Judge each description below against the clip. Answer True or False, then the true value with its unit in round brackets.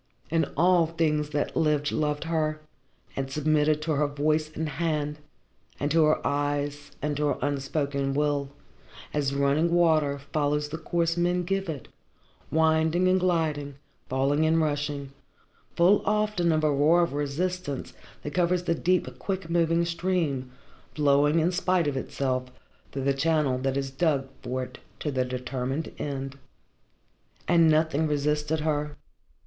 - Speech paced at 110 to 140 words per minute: False (150 wpm)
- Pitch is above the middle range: False (150 Hz)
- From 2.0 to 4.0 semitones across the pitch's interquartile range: True (2.7 semitones)